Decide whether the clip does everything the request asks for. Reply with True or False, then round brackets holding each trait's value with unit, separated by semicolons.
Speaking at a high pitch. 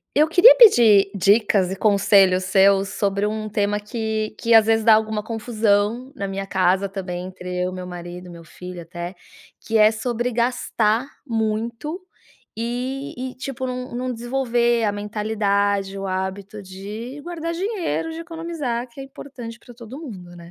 True (215 Hz)